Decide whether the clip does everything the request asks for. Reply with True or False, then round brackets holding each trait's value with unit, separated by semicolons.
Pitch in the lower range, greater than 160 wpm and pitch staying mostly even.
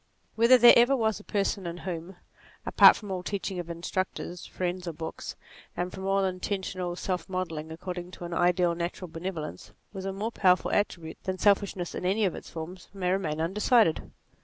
False (185 Hz; 190 wpm; 2.2 semitones)